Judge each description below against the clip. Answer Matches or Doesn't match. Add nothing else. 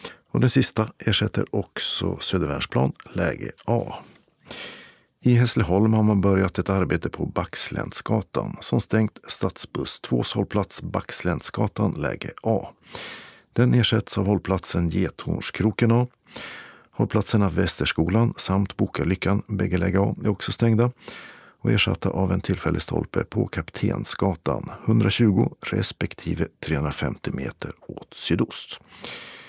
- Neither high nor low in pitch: Doesn't match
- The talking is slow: Matches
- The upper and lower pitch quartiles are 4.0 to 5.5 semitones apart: Doesn't match